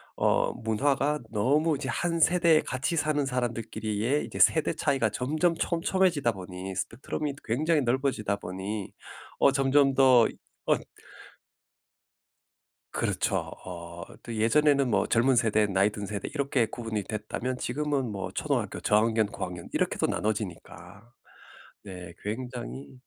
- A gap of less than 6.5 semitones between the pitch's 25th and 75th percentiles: Yes, average, 5.2 semitones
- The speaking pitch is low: Yes, low, 120 Hz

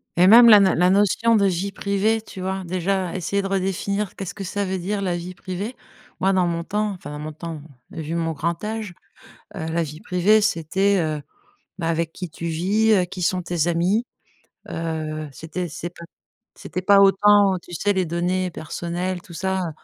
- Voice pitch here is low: No, medium, 185 Hz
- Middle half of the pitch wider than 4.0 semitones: No, average, 2.9 semitones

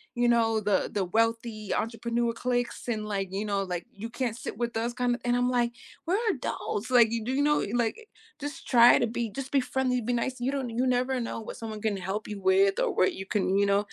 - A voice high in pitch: Yes, high, 235 Hz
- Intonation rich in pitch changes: No, average, 2.9 semitones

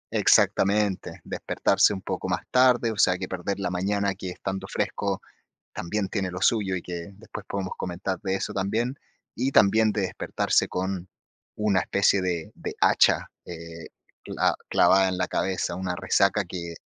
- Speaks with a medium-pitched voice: No, very low, 95 Hz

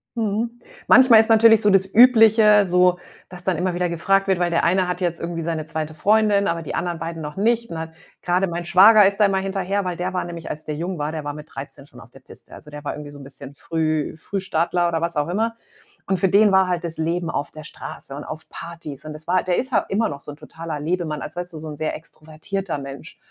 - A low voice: No, medium, 175 Hz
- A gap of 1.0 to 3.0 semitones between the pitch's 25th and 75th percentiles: No, average, 3.8 semitones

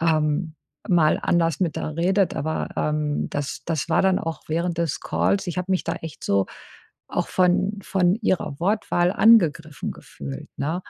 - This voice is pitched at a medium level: Yes, medium, 170 Hz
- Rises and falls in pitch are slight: No, average, 3.2 semitones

